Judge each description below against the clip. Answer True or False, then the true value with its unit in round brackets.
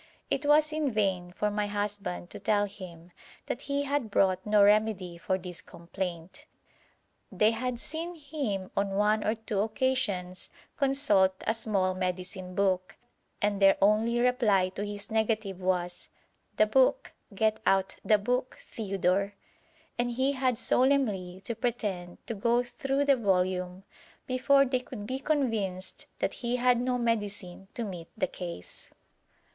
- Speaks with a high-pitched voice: True (210 Hz)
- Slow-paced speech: False (150 wpm)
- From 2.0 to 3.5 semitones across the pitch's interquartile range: False (4.9 semitones)